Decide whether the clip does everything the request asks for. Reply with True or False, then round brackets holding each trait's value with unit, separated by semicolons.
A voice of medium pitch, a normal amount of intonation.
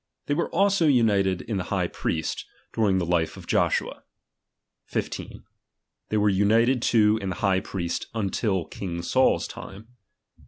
False (100 Hz; 3.3 semitones)